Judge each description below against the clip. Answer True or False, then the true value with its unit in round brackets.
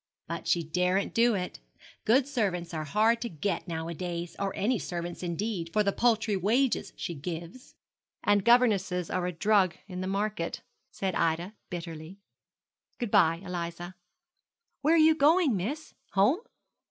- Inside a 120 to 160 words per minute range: True (150 wpm)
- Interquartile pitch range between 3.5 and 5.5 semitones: True (4.7 semitones)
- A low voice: False (190 Hz)